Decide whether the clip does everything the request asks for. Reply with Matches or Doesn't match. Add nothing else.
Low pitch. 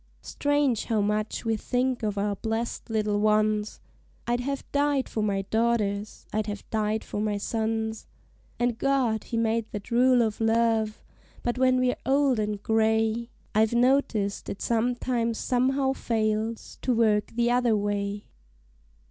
Doesn't match